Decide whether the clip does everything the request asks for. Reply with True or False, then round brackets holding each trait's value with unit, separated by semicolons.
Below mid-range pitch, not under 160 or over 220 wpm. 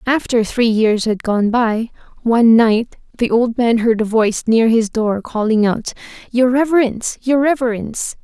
False (230 Hz; 170 wpm)